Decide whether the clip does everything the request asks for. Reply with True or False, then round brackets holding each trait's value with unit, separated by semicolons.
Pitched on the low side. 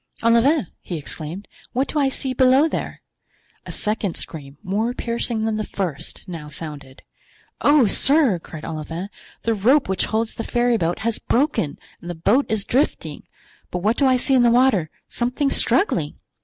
False (220 Hz)